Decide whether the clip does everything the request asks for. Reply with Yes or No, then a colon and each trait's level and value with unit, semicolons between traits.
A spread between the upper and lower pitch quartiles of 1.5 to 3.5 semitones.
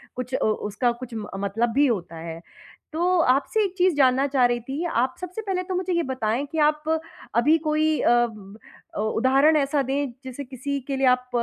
No: average, 4.3 semitones